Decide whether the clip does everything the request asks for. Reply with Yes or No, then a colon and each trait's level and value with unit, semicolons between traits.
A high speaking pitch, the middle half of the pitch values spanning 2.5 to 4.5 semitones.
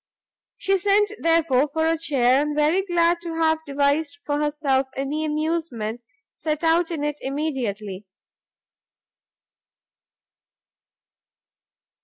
Yes: very high, 300 Hz; average, 3.1 semitones